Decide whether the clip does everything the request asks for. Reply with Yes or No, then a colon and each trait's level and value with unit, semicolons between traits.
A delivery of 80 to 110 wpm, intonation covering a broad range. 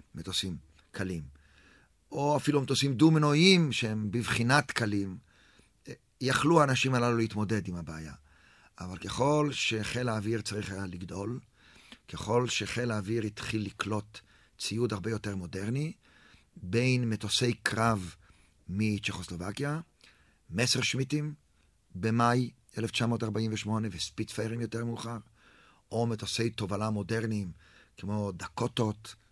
No: slow, 100 wpm; average, 3.4 semitones